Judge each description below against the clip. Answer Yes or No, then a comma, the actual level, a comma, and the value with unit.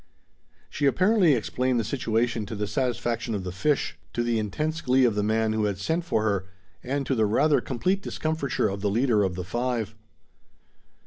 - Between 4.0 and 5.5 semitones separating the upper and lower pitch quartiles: Yes, average, 4.8 semitones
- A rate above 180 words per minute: Yes, average, 190 wpm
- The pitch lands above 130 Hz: No, low, 120 Hz